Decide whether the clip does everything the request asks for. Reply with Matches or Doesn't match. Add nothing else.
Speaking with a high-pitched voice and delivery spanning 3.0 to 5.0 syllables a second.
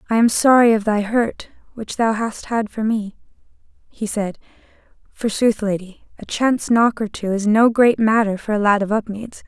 Matches